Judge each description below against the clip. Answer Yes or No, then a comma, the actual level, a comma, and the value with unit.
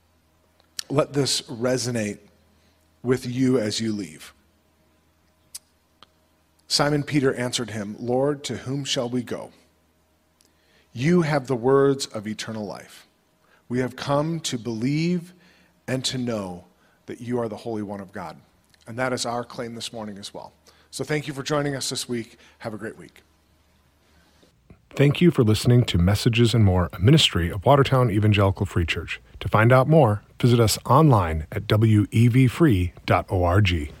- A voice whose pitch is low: Yes, low, 110 Hz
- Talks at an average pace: Yes, average, 150 wpm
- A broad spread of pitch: Yes, wide, 6.9 semitones